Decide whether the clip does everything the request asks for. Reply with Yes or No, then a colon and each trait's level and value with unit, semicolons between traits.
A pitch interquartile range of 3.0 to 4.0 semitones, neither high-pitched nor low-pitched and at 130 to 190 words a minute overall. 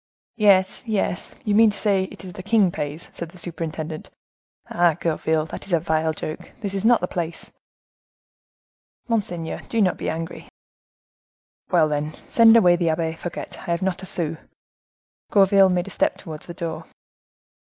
Yes: average, 3.4 semitones; medium, 175 Hz; average, 170 wpm